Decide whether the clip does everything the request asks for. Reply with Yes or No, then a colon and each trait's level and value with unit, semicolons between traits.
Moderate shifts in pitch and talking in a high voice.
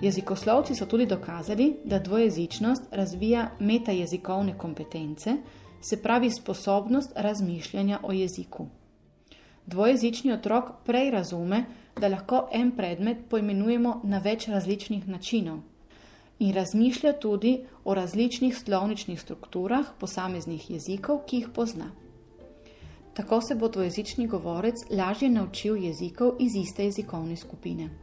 Yes: average, 4.4 semitones; high, 205 Hz